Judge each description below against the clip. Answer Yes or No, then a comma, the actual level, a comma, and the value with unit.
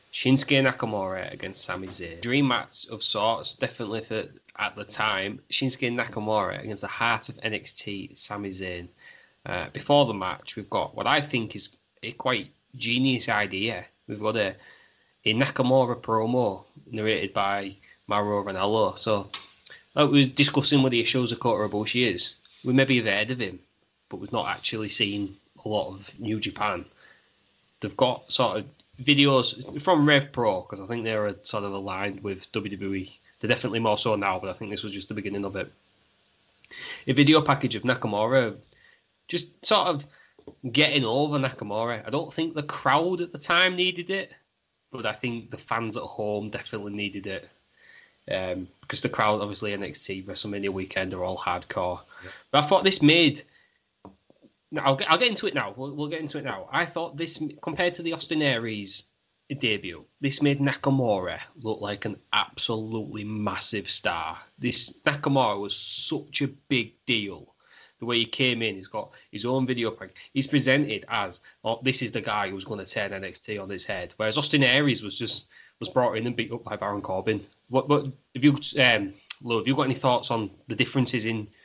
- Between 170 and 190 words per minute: Yes, average, 185 wpm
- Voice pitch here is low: Yes, low, 115 Hz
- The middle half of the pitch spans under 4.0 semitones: No, average, 5.1 semitones